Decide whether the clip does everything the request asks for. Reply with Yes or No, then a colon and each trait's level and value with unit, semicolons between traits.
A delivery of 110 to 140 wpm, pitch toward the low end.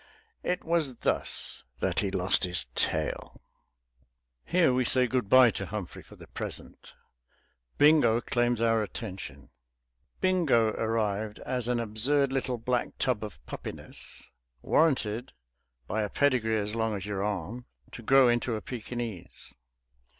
Yes: slow, 135 wpm; low, 115 Hz